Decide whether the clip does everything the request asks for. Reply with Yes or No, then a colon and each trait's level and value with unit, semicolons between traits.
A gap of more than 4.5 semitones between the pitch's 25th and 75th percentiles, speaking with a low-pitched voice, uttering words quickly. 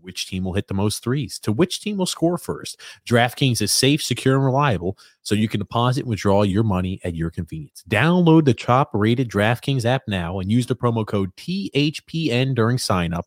Yes: average, 5.2 semitones; low, 120 Hz; fast, 210 wpm